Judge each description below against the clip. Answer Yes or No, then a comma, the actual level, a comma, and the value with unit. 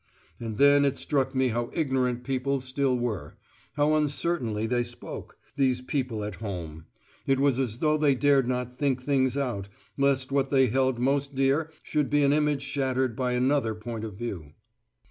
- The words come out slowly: No, average, 175 wpm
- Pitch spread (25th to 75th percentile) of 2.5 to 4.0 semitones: Yes, average, 2.8 semitones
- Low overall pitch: Yes, low, 130 Hz